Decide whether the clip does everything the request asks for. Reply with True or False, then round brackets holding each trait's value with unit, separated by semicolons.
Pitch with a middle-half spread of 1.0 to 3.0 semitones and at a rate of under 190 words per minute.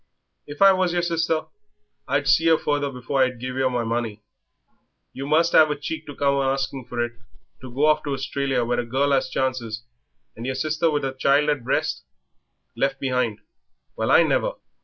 False (2.7 semitones; 200 wpm)